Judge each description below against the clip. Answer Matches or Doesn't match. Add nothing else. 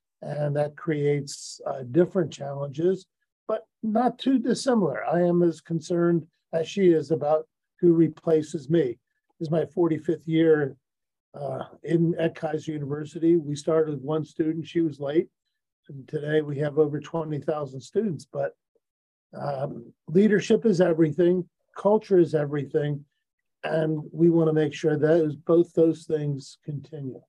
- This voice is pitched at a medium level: Matches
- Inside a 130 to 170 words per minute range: Matches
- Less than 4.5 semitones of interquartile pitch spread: Matches